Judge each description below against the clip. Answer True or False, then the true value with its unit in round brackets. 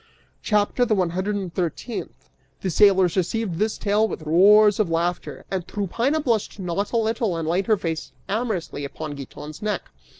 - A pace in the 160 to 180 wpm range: True (170 wpm)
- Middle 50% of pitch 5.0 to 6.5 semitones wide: False (4.0 semitones)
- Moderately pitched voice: False (195 Hz)